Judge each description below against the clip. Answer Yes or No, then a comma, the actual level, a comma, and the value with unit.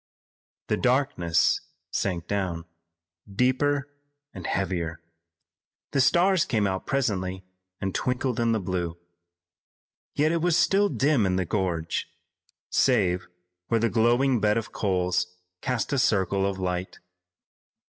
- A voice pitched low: Yes, low, 105 Hz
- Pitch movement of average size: No, wide, 6.0 semitones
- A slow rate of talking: Yes, slow, 125 wpm